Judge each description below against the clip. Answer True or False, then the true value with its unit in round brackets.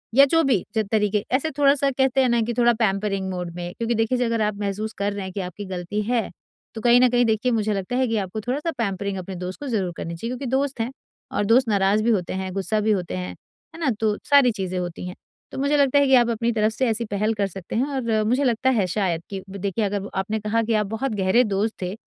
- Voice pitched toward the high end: True (215 Hz)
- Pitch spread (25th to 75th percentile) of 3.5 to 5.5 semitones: True (3.9 semitones)